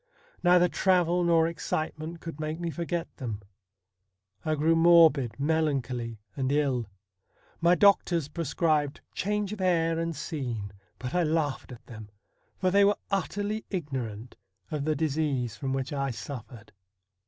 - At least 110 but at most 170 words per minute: Yes, average, 140 wpm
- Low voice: No, medium, 155 Hz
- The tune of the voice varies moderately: Yes, average, 4.4 semitones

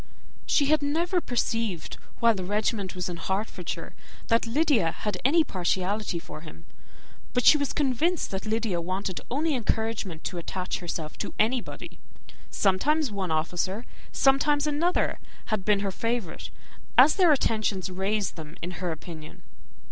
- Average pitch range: No, wide, 6.7 semitones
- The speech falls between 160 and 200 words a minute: No, average, 150 wpm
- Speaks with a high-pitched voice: Yes, high, 210 Hz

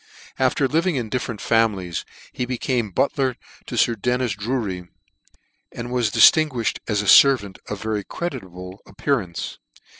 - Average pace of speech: No, slow, 130 wpm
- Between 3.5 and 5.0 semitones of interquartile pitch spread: Yes, average, 4.3 semitones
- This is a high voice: No, low, 115 Hz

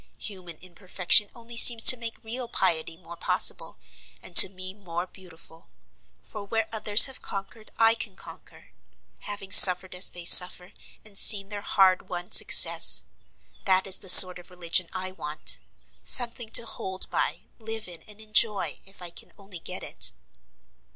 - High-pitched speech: Yes, high, 195 Hz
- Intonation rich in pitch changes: No, average, 3.3 semitones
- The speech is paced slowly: No, average, 160 wpm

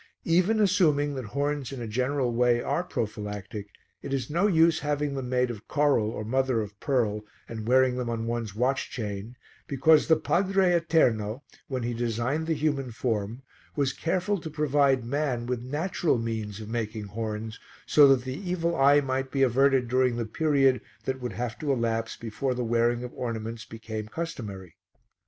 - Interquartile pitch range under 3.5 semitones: No, average, 4.3 semitones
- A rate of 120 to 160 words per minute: No, average, 175 wpm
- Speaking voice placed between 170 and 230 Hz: No, low, 125 Hz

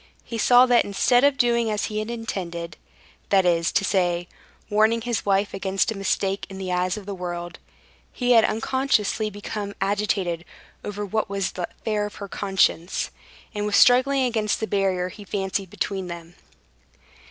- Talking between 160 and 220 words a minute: Yes, average, 165 wpm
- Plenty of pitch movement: No, average, 2.8 semitones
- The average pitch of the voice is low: No, high, 200 Hz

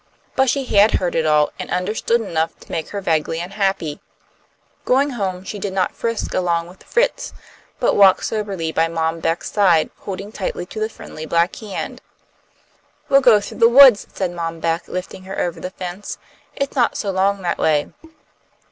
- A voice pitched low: No, high, 190 Hz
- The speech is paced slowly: No, average, 180 wpm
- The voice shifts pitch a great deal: No, average, 4.1 semitones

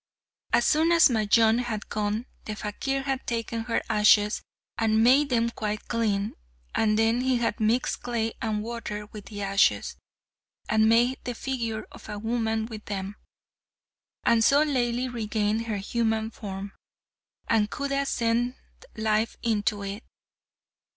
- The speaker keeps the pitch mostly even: Yes, narrow, 2.2 semitones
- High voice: Yes, high, 225 Hz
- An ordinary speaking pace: Yes, average, 145 wpm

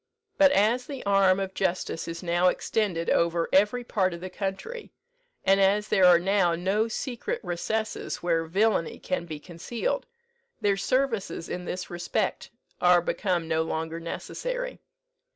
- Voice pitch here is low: No, high, 190 Hz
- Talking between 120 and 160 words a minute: Yes, average, 150 wpm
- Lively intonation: No, average, 3.9 semitones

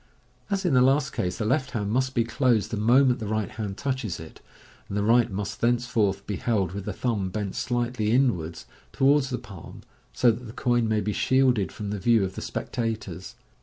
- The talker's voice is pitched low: Yes, low, 115 Hz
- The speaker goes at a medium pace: No, fast, 210 wpm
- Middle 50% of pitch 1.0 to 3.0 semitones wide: No, average, 3.7 semitones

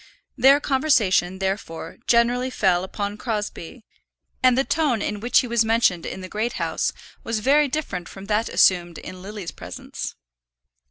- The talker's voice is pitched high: Yes, high, 215 Hz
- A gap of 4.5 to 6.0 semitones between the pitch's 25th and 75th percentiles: Yes, average, 4.8 semitones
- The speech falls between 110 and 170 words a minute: Yes, average, 155 wpm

